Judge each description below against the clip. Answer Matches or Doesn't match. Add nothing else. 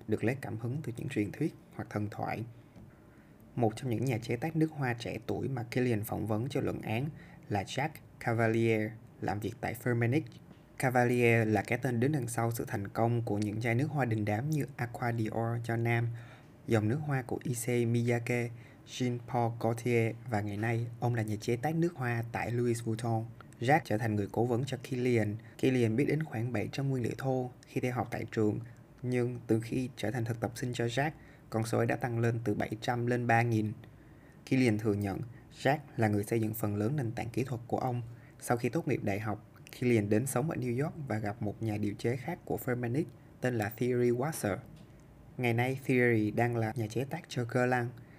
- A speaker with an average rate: Matches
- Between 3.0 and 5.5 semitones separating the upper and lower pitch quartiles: Doesn't match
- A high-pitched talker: Doesn't match